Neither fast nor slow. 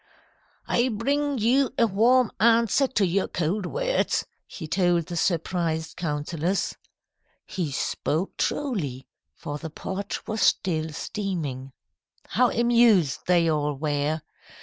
No: slow, 120 wpm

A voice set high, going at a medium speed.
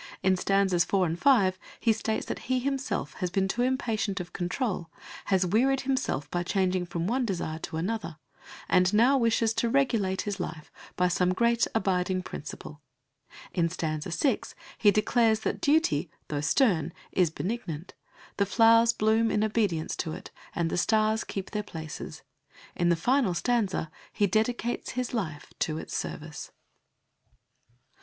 Yes: high, 195 Hz; average, 155 wpm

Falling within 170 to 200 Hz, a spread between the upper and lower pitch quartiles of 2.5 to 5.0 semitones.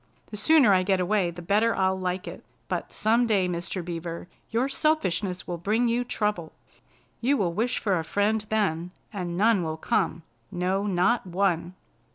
Yes: high, 190 Hz; average, 3.7 semitones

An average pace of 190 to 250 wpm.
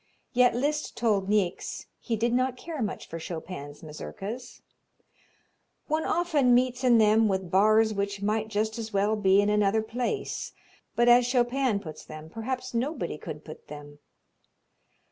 No: average, 155 wpm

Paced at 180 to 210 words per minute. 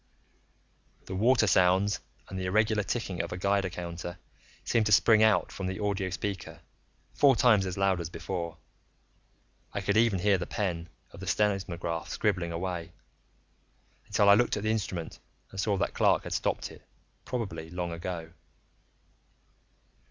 No: average, 155 wpm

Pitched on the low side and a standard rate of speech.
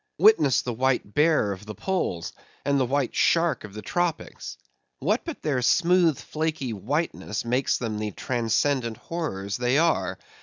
Yes: low, 130 Hz; average, 155 wpm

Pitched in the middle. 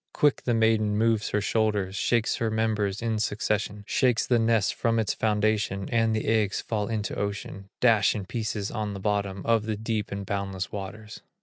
No: low, 110 Hz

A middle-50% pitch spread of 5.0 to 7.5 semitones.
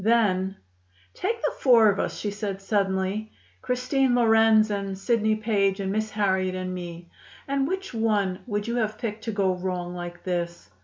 No: average, 3.0 semitones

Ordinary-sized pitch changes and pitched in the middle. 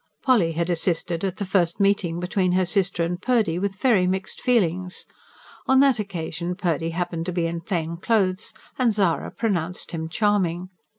Yes: average, 3.0 semitones; medium, 180 Hz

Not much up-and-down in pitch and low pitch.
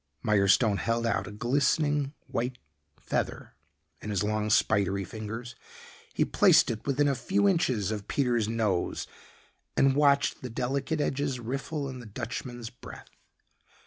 No: average, 4.5 semitones; low, 120 Hz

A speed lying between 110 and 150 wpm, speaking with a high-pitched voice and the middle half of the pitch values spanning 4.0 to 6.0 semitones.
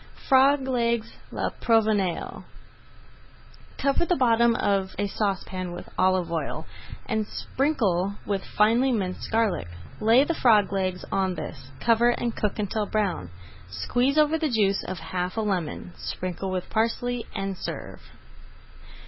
Yes: average, 140 wpm; high, 215 Hz; average, 4.3 semitones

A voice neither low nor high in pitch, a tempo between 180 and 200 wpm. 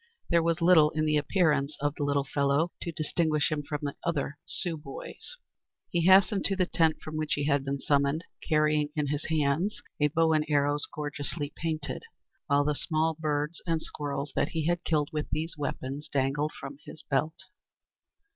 Yes: medium, 150 Hz; average, 185 wpm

